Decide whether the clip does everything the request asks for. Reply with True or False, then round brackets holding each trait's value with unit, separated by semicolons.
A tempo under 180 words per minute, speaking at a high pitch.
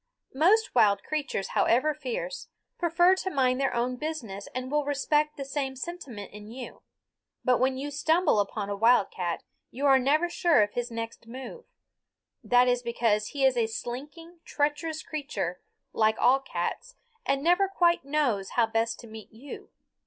True (165 wpm; 265 Hz)